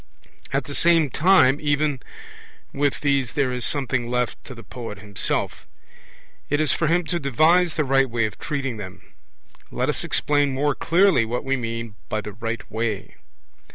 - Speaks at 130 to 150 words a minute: No, average, 170 wpm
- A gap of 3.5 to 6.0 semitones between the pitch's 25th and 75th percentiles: Yes, average, 4.2 semitones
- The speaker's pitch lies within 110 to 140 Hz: Yes, low, 135 Hz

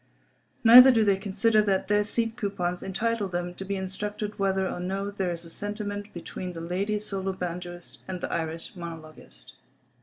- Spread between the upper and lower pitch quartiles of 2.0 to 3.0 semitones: Yes, average, 2.7 semitones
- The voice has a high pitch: Yes, high, 195 Hz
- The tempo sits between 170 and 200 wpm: Yes, average, 175 wpm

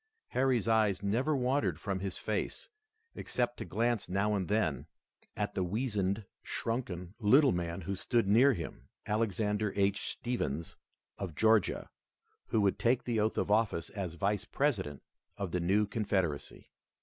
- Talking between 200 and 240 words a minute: No, average, 150 wpm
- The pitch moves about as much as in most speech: Yes, average, 3.4 semitones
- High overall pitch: No, low, 105 Hz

